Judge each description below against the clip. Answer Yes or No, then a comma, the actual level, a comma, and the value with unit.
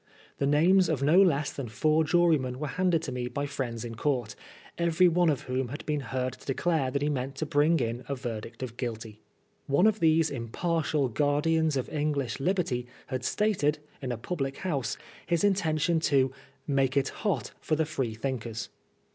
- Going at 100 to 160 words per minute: No, average, 190 wpm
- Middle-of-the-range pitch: Yes, medium, 145 Hz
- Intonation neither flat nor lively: Yes, average, 4.0 semitones